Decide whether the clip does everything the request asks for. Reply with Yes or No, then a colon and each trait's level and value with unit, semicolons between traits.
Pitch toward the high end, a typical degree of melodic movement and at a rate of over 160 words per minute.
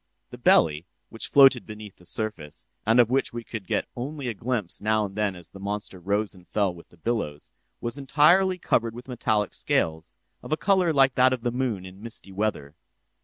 No: low, 110 Hz; average, 4.7 semitones; fast, 205 wpm